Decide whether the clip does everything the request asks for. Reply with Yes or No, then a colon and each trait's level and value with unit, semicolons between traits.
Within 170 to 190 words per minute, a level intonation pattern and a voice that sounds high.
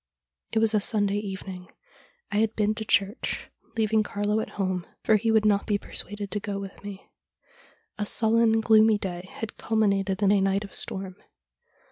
Yes: average, 175 wpm; narrow, 1.9 semitones; high, 205 Hz